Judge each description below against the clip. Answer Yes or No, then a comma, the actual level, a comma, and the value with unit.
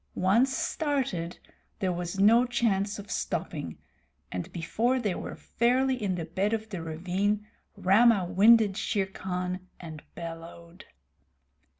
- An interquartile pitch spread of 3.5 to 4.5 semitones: Yes, average, 4.2 semitones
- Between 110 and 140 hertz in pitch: No, high, 195 Hz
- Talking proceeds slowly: Yes, slow, 125 wpm